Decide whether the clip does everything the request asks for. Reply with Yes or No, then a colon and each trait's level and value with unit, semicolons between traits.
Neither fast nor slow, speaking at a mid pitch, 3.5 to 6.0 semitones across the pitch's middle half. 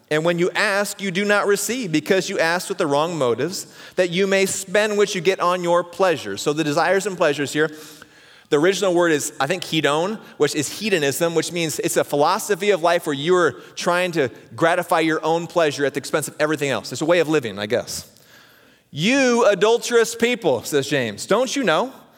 No: fast, 210 wpm; medium, 175 Hz; average, 4.4 semitones